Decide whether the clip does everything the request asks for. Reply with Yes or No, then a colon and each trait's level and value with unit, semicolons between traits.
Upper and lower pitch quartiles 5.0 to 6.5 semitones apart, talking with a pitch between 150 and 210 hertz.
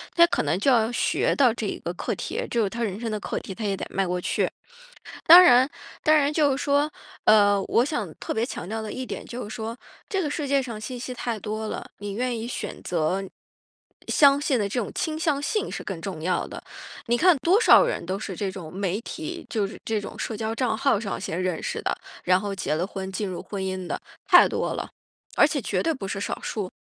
No: wide, 5.5 semitones; high, 220 Hz